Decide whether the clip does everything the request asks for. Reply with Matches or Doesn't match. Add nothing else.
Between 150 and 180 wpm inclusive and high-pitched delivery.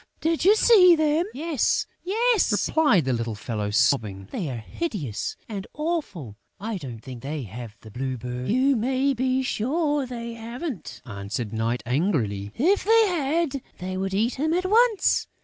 Matches